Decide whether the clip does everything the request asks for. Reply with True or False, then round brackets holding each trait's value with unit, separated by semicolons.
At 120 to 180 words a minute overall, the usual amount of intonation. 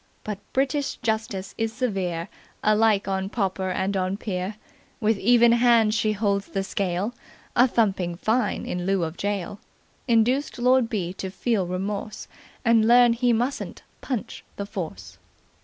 True (145 wpm; 3.5 semitones)